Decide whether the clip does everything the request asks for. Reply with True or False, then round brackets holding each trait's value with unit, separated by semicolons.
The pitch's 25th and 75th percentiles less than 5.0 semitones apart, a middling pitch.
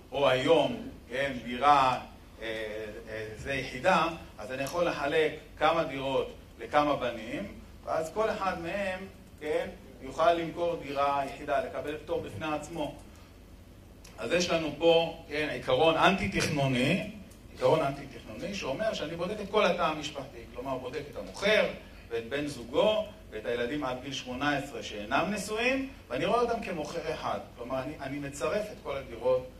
False (5.5 semitones; 150 Hz)